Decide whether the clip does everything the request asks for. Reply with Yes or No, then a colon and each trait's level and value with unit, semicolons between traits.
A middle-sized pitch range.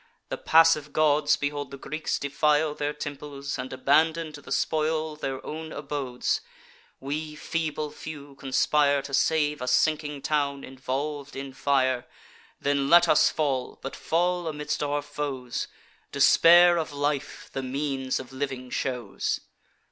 No: narrow, 2.0 semitones